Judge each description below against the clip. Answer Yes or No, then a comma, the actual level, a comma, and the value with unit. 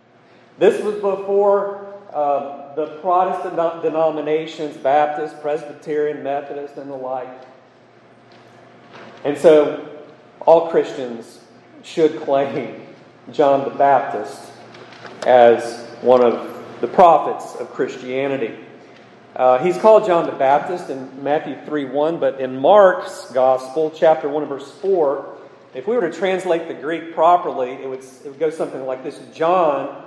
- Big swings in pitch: No, average, 4.0 semitones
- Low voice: No, medium, 150 Hz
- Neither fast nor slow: No, slow, 125 wpm